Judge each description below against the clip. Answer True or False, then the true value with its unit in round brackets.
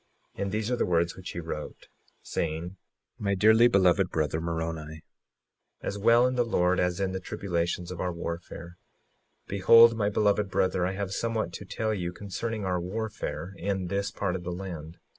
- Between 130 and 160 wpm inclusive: False (180 wpm)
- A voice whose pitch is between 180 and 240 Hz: False (95 Hz)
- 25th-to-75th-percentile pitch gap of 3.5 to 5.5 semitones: False (3.0 semitones)